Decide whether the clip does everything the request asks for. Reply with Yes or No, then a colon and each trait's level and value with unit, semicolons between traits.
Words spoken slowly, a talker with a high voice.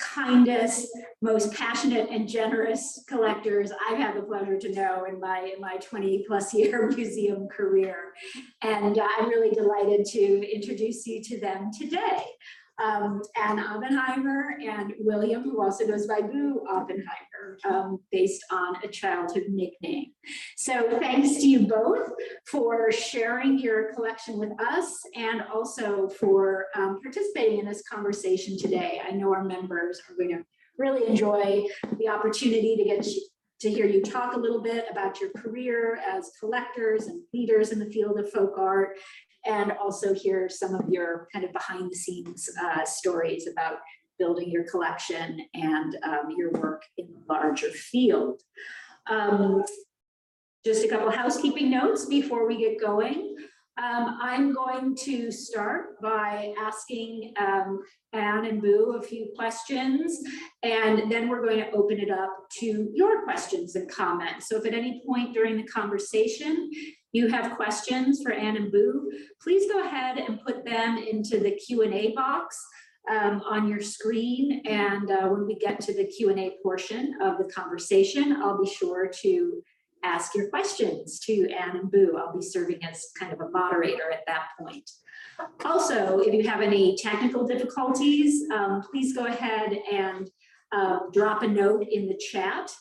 No: average, 160 wpm; high, 220 Hz